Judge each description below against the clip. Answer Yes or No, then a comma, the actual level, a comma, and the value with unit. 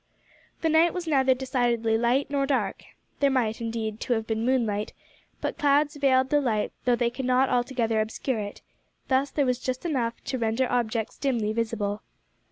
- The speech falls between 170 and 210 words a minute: Yes, average, 175 wpm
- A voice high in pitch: Yes, high, 245 Hz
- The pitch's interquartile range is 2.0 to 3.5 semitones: Yes, average, 3.1 semitones